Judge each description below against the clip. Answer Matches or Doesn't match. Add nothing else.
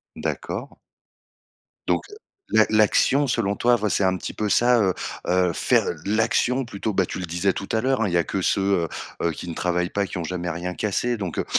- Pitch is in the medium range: Doesn't match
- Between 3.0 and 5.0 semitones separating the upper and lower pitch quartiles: Matches